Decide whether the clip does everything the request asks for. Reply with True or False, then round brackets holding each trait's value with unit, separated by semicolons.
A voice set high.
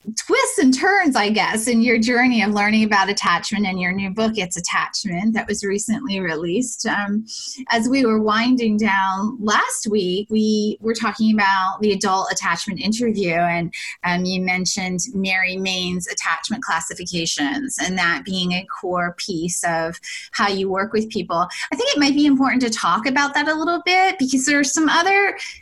True (210 Hz)